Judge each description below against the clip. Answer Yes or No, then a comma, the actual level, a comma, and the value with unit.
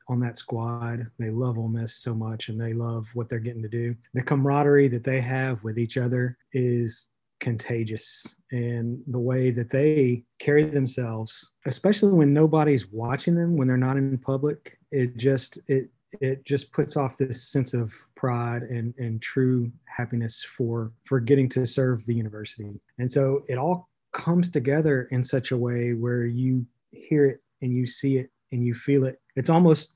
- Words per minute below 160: No, average, 180 wpm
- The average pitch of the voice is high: No, low, 125 Hz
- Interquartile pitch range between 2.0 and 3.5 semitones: Yes, narrow, 2.5 semitones